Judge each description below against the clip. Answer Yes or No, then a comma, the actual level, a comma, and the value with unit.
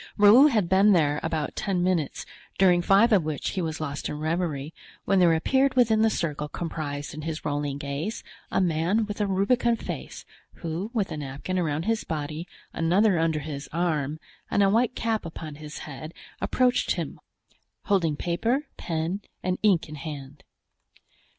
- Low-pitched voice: No, medium, 170 Hz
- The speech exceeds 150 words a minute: Yes, average, 170 wpm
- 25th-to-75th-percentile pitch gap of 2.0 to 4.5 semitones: No, average, 5.0 semitones